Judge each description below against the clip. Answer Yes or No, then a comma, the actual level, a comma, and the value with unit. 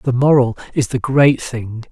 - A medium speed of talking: Yes, average, 190 wpm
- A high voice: No, low, 125 Hz